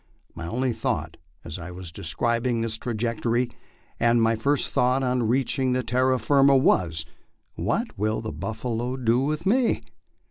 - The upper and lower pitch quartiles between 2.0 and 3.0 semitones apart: Yes, average, 2.7 semitones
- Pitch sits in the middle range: No, low, 120 Hz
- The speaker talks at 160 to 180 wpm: No, average, 150 wpm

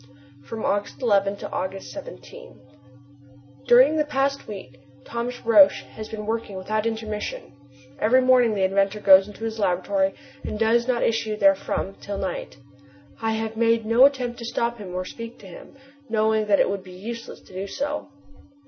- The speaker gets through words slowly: No, average, 170 wpm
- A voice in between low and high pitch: No, high, 220 Hz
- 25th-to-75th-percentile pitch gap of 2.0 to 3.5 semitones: Yes, average, 3.1 semitones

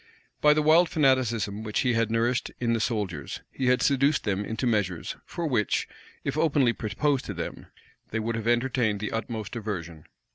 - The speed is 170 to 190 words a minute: Yes, average, 180 wpm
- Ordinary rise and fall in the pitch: Yes, average, 3.8 semitones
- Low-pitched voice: Yes, low, 115 Hz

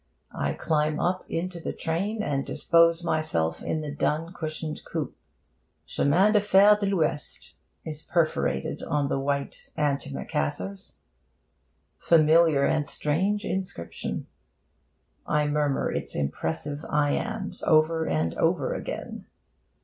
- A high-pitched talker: No, medium, 155 Hz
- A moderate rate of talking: No, slow, 115 wpm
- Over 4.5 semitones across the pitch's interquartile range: No, average, 3.0 semitones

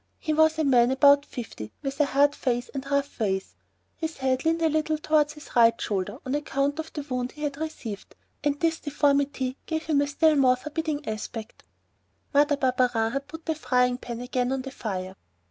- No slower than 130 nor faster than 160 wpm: No, average, 200 wpm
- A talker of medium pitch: No, very high, 280 Hz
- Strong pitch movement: No, average, 3.4 semitones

